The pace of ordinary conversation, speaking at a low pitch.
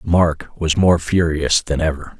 Yes: average, 165 wpm; very low, 80 Hz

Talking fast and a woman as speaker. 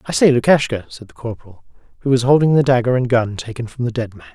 No: fast, 250 wpm; male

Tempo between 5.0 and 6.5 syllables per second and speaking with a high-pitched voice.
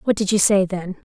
Yes: 5.4 syllables/s; high, 195 Hz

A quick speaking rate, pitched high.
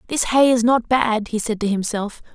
Yes: fast, 230 wpm; high, 230 Hz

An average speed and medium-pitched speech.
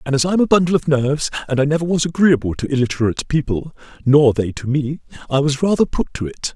No: fast, 230 wpm; medium, 145 Hz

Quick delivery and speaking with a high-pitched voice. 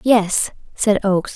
No: slow, 135 wpm; high, 205 Hz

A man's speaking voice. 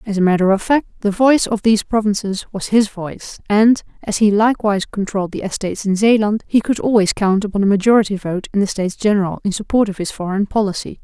No: female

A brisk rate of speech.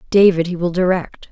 No: average, 180 wpm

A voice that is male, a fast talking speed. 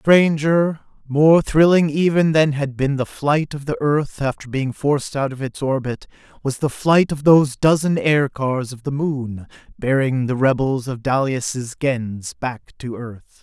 No: male; average, 170 wpm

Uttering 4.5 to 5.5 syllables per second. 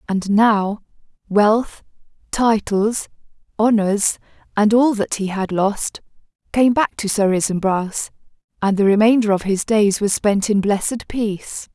No: 4.1 syllables/s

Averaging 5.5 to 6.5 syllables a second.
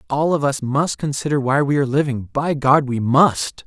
No: 4.9 syllables/s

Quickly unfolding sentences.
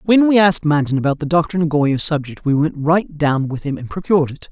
Yes: fast, 240 wpm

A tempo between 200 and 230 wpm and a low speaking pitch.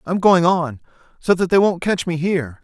No: fast, 205 wpm; medium, 170 Hz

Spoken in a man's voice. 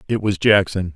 Yes: male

